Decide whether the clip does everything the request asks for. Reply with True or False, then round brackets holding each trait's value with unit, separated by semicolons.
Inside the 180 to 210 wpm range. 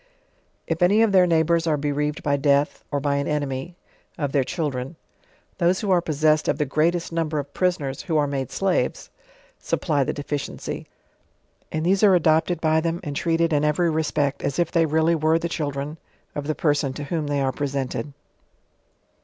True (185 wpm)